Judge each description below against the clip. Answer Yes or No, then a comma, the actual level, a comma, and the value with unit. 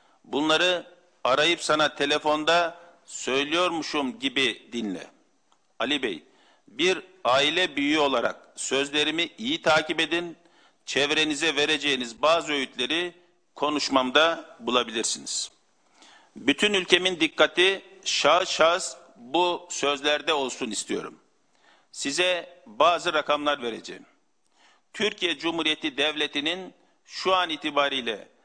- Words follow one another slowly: Yes, slow, 90 wpm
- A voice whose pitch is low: No, medium, 165 Hz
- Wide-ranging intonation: No, average, 3.2 semitones